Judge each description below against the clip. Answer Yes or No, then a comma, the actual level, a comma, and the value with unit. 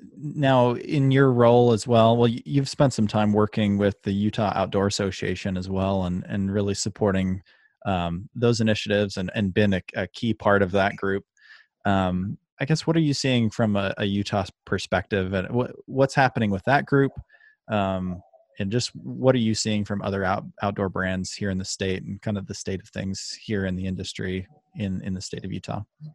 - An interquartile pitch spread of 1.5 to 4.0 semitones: Yes, average, 3.7 semitones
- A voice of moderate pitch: No, low, 100 Hz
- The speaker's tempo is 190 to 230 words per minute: Yes, average, 200 wpm